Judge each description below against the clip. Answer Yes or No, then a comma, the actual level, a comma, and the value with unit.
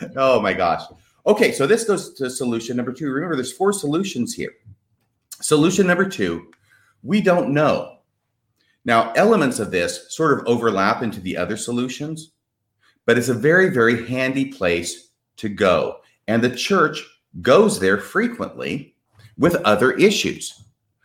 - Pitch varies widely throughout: Yes, wide, 6.3 semitones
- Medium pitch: No, low, 125 Hz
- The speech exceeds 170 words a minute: No, average, 145 wpm